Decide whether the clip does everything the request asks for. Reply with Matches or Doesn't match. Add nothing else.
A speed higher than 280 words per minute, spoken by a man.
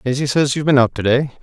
Matches